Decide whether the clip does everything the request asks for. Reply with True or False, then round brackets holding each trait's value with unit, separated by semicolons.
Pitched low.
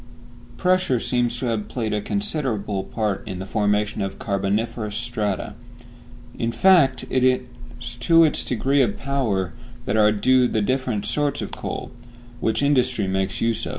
True (115 Hz)